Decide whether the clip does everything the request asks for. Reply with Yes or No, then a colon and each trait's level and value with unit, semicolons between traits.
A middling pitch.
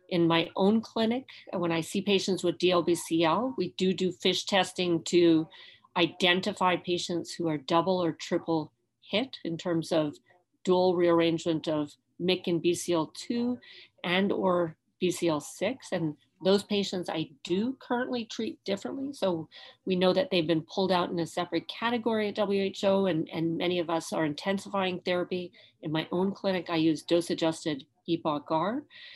Yes: medium, 180 Hz